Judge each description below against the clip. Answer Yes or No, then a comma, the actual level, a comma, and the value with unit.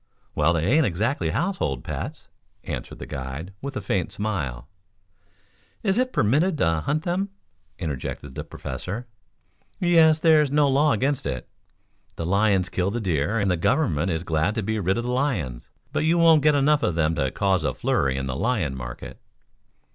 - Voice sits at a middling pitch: No, low, 100 Hz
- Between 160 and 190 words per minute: Yes, average, 175 wpm